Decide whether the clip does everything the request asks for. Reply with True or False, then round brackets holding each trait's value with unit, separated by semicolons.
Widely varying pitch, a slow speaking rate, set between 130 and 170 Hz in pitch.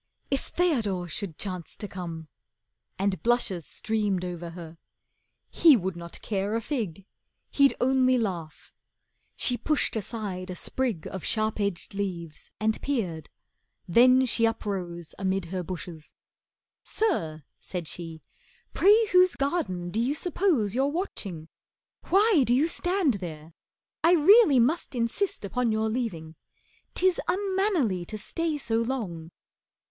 False (7.6 semitones; 130 wpm; 215 Hz)